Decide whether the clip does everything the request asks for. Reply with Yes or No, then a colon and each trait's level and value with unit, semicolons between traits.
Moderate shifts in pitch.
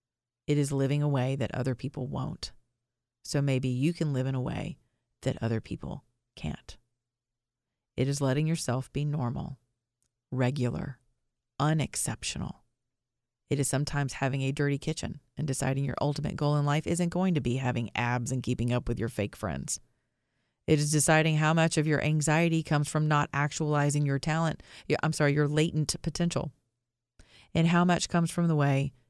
Yes: average, 3.8 semitones